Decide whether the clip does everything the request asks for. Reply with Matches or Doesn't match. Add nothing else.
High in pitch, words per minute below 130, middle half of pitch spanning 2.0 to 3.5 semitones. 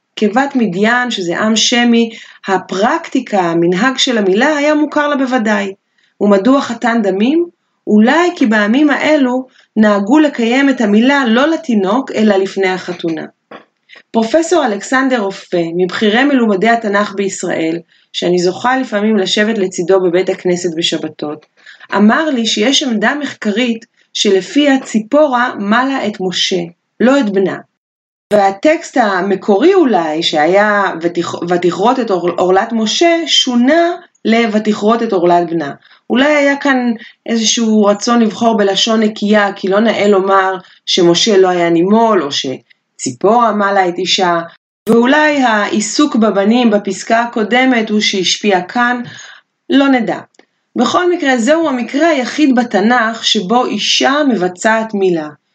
Doesn't match